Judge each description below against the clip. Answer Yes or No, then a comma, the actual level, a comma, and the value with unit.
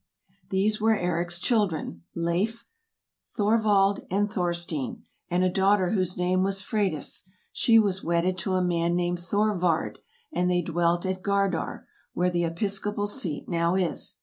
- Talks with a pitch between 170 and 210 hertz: Yes, medium, 185 Hz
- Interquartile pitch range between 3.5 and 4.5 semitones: No, average, 2.7 semitones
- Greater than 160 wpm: No, average, 145 wpm